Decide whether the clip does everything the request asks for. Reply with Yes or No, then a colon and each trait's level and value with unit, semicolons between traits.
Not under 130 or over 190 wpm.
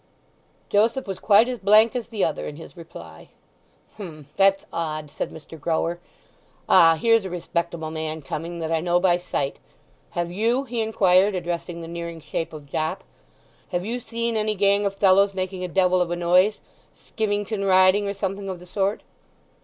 Yes: average, 170 wpm